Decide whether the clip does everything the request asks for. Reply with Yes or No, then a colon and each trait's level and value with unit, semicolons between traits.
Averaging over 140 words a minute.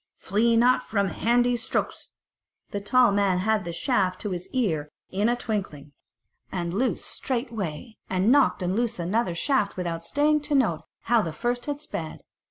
Yes: average, 170 wpm